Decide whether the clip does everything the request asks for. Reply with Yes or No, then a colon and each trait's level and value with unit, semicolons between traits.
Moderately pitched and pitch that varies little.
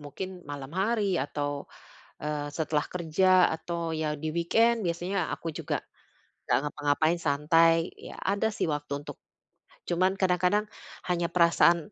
No: medium, 170 Hz; average, 3.6 semitones